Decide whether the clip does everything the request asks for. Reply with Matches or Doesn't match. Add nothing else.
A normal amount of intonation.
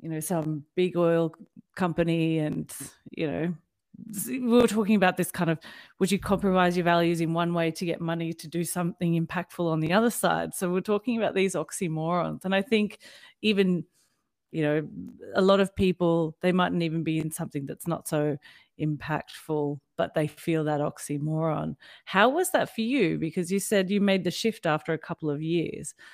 Matches